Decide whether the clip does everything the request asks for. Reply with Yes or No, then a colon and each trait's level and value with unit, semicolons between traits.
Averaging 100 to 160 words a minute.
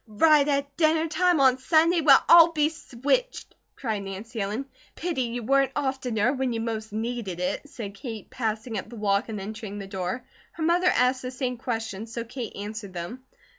No: average, 185 wpm